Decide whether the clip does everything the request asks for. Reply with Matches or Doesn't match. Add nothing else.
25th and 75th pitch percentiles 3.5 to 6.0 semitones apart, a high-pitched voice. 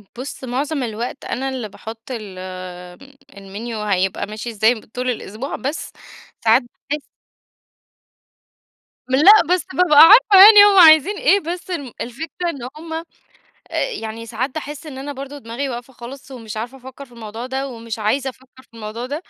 Matches